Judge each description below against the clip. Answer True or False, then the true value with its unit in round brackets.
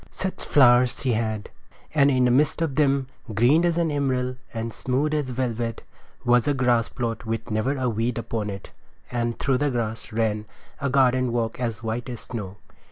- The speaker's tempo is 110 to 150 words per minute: False (190 wpm)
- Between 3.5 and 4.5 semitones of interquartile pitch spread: False (3.0 semitones)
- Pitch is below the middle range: True (125 Hz)